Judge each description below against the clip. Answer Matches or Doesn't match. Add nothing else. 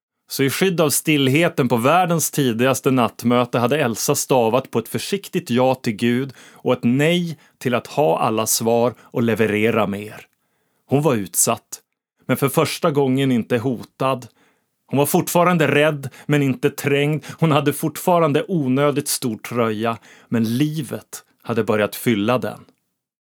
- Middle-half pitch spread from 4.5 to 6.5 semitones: Doesn't match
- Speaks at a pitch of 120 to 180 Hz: Matches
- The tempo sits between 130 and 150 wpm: Matches